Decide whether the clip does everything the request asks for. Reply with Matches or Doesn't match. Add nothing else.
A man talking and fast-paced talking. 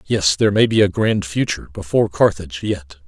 Doesn't match